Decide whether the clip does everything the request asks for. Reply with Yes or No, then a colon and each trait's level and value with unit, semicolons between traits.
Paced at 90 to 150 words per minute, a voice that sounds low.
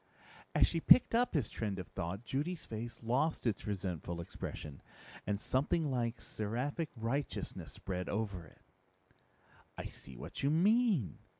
Yes: average, 140 wpm; low, 115 Hz